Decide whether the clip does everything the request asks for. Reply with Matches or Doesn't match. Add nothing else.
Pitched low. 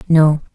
Doesn't match